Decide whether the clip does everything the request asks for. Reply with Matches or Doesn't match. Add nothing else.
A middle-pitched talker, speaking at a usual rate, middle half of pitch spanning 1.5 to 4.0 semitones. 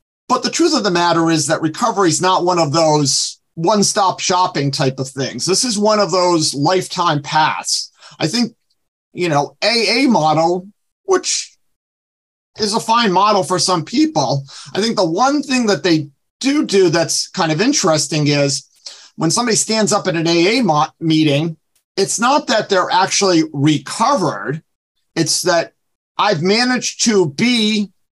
Doesn't match